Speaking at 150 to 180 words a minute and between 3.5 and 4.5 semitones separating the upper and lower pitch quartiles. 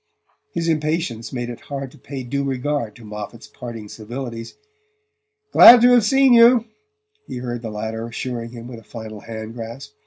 Yes: average, 175 wpm; average, 4.0 semitones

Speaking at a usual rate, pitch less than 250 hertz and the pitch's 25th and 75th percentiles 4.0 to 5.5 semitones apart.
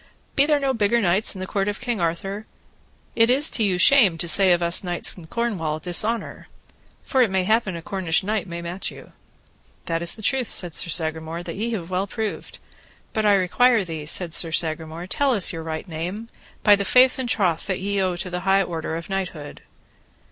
No: fast, 210 wpm; high, 190 Hz; average, 4.3 semitones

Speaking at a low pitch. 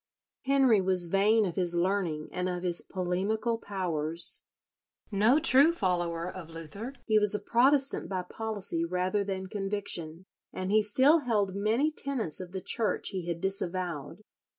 No: high, 195 Hz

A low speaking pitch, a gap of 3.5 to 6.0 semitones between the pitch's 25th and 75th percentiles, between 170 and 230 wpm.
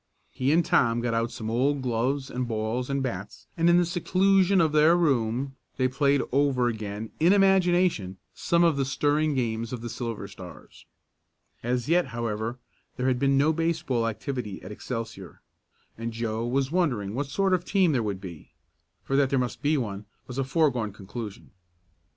Yes: low, 130 Hz; average, 5.0 semitones; average, 180 wpm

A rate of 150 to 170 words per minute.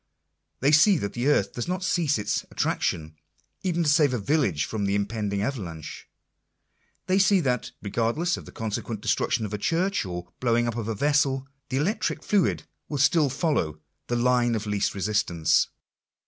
No: average, 180 wpm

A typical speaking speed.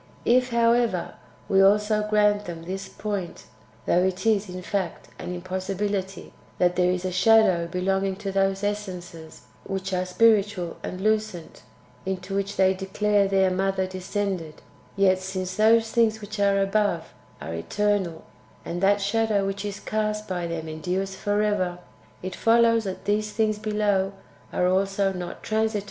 Yes: average, 155 wpm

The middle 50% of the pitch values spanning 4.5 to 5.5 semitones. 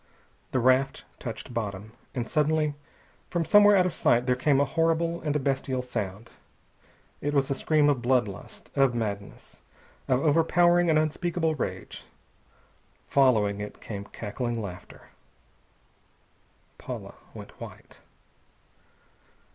Yes: average, 5.1 semitones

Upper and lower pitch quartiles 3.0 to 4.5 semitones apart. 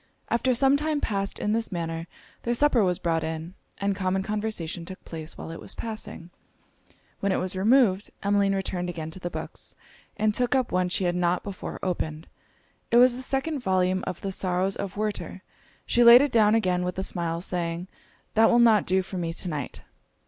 Yes: average, 4.1 semitones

